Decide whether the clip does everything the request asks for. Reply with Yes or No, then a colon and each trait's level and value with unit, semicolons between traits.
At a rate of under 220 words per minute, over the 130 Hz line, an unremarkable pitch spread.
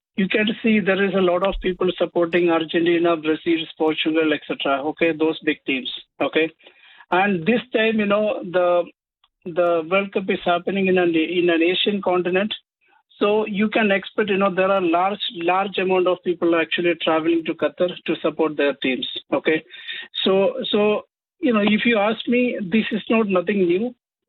Yes: average, 175 wpm; medium, 185 Hz; average, 3.7 semitones